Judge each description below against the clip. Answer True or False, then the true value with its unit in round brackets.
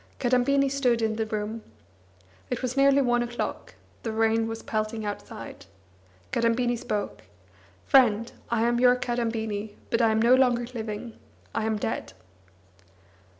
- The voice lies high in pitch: True (230 Hz)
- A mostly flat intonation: True (2.0 semitones)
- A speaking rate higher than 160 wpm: False (140 wpm)